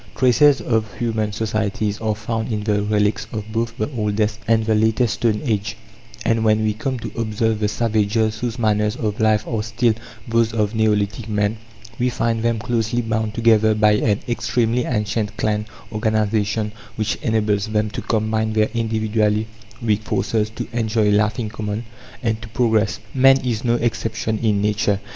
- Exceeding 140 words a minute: Yes, average, 170 wpm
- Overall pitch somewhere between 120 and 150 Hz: No, low, 110 Hz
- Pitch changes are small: Yes, narrow, 1.2 semitones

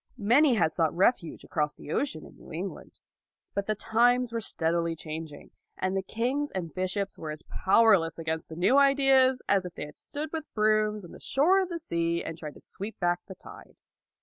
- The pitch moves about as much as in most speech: No, wide, 7.0 semitones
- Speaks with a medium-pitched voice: No, high, 195 Hz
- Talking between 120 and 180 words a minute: No, average, 200 wpm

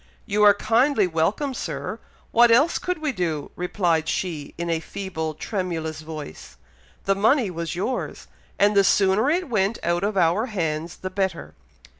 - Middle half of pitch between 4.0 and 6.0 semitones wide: Yes, average, 4.8 semitones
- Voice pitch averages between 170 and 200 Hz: Yes, high, 190 Hz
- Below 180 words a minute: Yes, average, 160 wpm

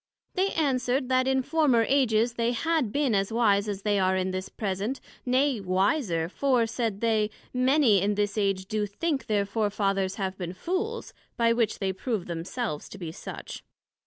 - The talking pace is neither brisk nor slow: Yes, average, 180 wpm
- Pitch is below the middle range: No, high, 220 Hz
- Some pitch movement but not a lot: Yes, average, 4.7 semitones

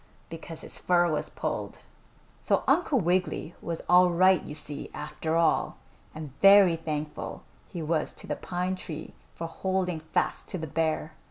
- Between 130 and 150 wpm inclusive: No, average, 160 wpm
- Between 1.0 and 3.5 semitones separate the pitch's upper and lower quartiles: Yes, narrow, 2.4 semitones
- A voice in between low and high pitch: Yes, medium, 165 Hz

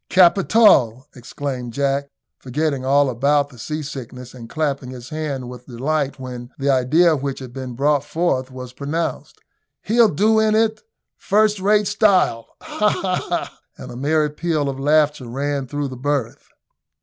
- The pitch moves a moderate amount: Yes, average, 3.7 semitones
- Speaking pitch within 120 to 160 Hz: Yes, medium, 140 Hz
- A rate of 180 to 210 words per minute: No, average, 155 wpm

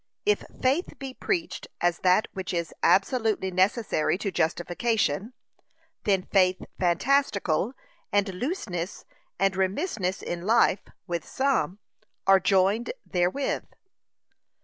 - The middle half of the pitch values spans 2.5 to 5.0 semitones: Yes, average, 4.7 semitones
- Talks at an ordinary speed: No, slow, 105 wpm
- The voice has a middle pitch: No, high, 195 Hz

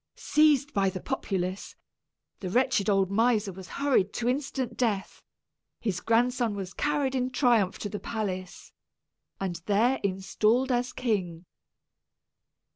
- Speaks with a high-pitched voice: Yes, high, 220 Hz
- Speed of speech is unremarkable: No, slow, 125 wpm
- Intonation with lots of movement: No, average, 4.7 semitones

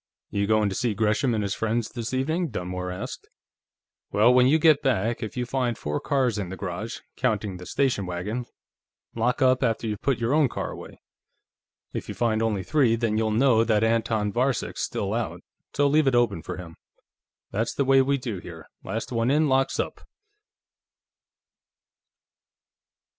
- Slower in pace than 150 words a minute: No, average, 175 wpm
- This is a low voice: Yes, low, 115 Hz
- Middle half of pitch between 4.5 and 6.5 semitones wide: No, average, 3.8 semitones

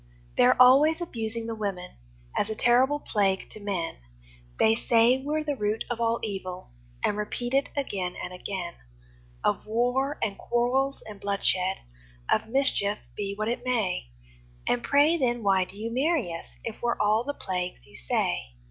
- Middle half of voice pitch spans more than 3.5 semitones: Yes, average, 4.3 semitones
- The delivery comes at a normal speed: Yes, average, 165 wpm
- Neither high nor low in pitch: No, high, 225 Hz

